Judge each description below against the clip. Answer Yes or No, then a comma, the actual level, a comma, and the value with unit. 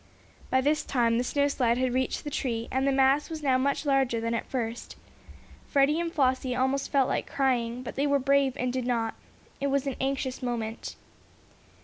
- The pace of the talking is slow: No, average, 190 wpm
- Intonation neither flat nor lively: No, narrow, 2.3 semitones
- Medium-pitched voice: No, very high, 260 Hz